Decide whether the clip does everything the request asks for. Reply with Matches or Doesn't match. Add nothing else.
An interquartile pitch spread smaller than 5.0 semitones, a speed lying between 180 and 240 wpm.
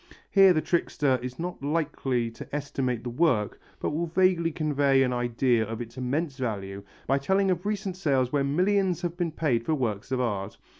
Doesn't match